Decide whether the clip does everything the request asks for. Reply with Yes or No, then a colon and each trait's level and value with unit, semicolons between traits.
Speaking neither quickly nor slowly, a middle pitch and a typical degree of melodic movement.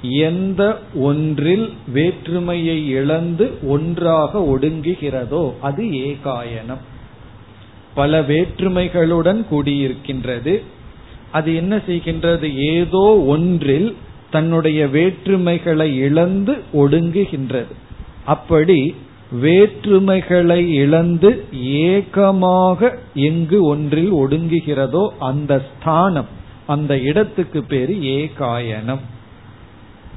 No: slow, 65 wpm; medium, 155 Hz; average, 4.6 semitones